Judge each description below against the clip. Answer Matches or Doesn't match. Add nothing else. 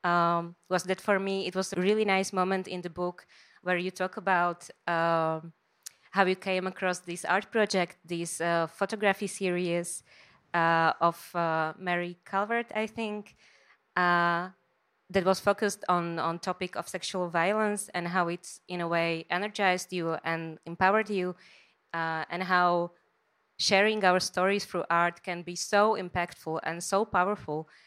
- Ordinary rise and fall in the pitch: Doesn't match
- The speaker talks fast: Doesn't match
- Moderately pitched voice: Matches